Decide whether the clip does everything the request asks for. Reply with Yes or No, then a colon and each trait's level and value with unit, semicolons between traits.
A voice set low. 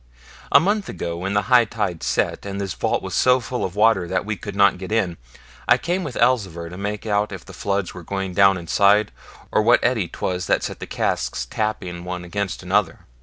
Yes: low, 100 Hz